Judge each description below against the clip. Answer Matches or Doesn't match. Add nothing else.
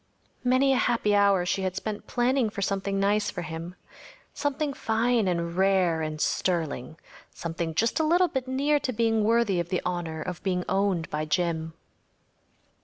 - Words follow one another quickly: Doesn't match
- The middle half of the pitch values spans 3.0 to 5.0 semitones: Doesn't match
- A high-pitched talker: Matches